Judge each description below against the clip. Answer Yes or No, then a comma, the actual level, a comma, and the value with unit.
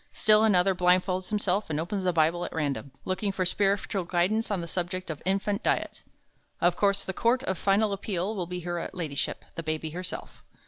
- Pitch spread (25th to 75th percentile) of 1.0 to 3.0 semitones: Yes, narrow, 2.5 semitones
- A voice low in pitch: No, medium, 185 Hz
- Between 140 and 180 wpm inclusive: No, average, 190 wpm